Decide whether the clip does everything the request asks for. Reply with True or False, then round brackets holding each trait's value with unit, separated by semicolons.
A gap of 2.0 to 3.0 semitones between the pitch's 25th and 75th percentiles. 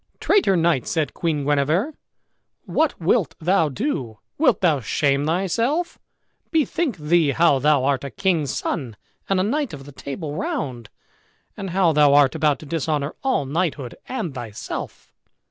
False (5.3 semitones)